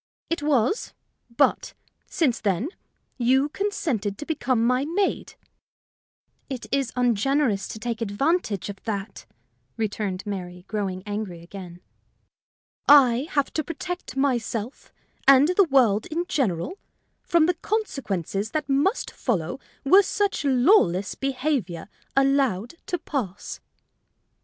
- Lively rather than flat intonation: Yes, wide, 6.5 semitones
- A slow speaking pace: Yes, slow, 115 wpm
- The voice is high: Yes, very high, 250 Hz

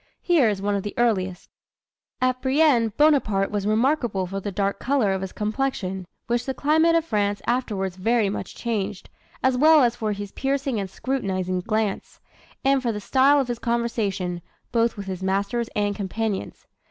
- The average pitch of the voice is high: Yes, high, 220 Hz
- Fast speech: No, average, 175 wpm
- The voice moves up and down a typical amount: Yes, average, 4.7 semitones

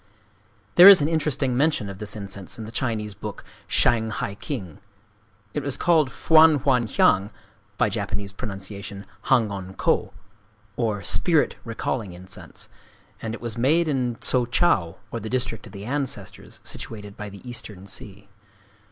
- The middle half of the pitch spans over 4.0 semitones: Yes, average, 4.9 semitones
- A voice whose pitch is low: Yes, low, 110 Hz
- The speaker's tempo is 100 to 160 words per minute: Yes, average, 150 wpm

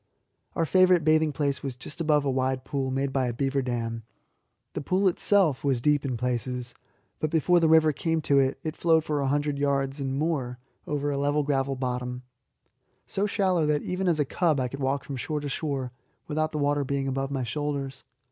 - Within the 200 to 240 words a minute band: Yes, fast, 205 wpm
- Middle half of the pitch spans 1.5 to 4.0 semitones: Yes, average, 2.7 semitones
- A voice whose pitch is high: No, medium, 140 Hz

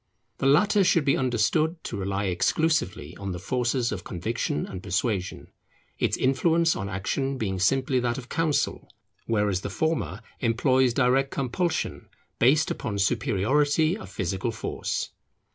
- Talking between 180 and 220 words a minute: No, average, 140 wpm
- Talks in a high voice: No, low, 125 Hz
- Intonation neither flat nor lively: No, wide, 6.5 semitones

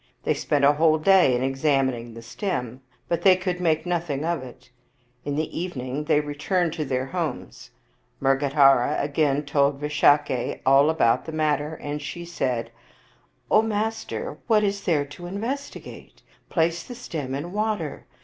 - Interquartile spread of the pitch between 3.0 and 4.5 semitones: Yes, average, 4.2 semitones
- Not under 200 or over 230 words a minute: No, average, 165 wpm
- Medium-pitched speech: Yes, medium, 150 Hz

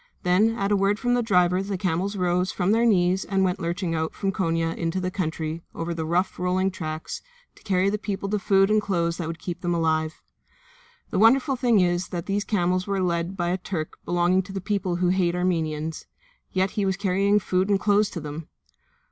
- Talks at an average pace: No, fast, 220 wpm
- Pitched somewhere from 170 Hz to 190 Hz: Yes, medium, 185 Hz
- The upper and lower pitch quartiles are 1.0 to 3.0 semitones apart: Yes, narrow, 2.5 semitones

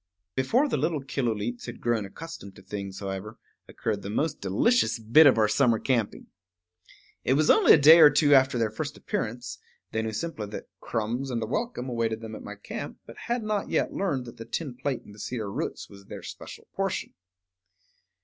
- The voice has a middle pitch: No, low, 120 Hz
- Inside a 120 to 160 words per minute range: No, average, 195 wpm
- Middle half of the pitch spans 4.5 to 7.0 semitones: Yes, average, 5.1 semitones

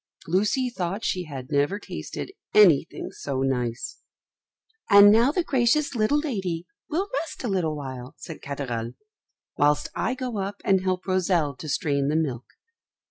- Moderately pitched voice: Yes, medium, 180 Hz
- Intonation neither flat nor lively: No, wide, 7.3 semitones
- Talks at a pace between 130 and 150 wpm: Yes, average, 145 wpm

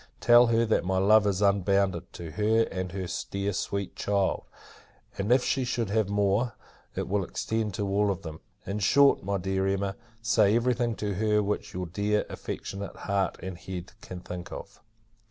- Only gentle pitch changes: Yes, narrow, 2.3 semitones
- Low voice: Yes, low, 100 Hz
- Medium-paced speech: Yes, average, 185 wpm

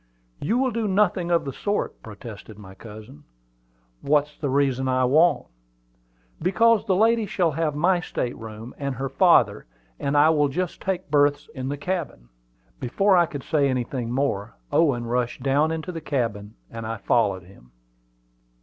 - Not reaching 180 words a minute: Yes, average, 165 wpm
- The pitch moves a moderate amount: No, wide, 6.3 semitones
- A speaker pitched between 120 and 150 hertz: Yes, medium, 140 Hz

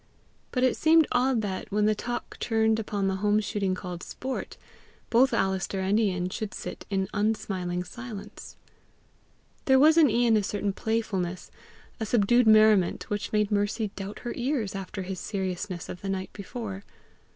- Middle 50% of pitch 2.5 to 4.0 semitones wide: Yes, average, 3.0 semitones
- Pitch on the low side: No, high, 210 Hz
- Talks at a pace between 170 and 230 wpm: No, average, 160 wpm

